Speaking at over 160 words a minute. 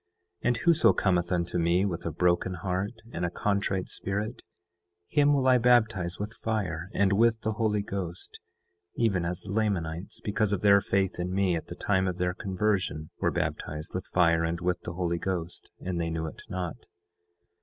Yes: average, 185 wpm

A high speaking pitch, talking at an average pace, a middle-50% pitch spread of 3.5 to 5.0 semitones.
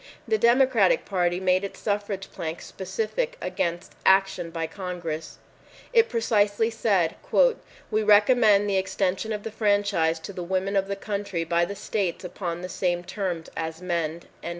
No: high, 195 Hz; average, 150 wpm; average, 3.0 semitones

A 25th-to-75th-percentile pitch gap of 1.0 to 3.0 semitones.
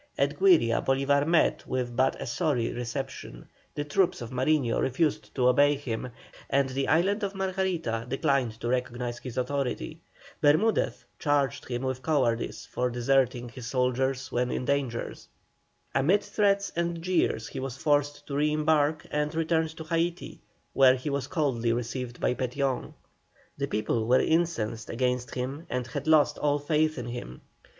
No: average, 3.9 semitones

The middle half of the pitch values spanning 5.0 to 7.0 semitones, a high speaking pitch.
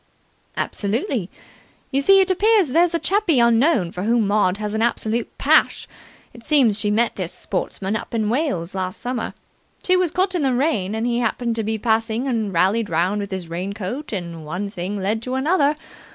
Yes: wide, 5.6 semitones; high, 225 Hz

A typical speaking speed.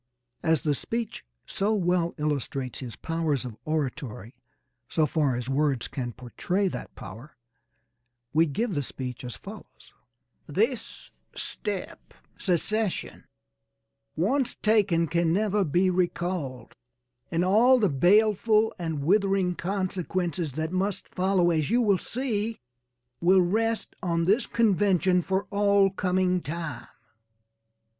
No: slow, 120 wpm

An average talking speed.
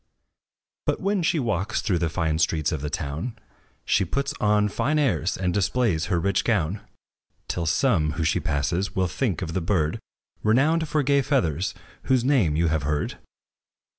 Yes: average, 170 wpm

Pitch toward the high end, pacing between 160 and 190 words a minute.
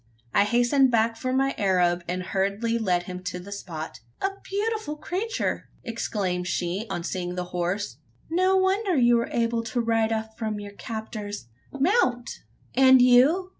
Yes: high, 225 Hz; average, 165 wpm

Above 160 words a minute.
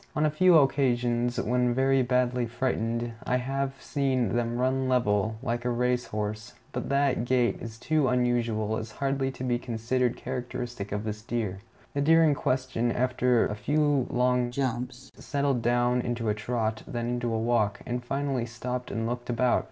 Yes: average, 175 wpm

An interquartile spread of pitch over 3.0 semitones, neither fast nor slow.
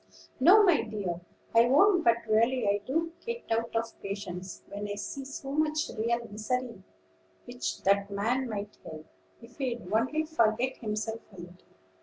Yes: average, 4.5 semitones; average, 160 wpm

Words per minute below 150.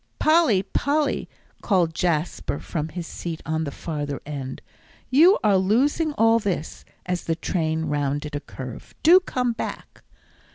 Yes: average, 140 wpm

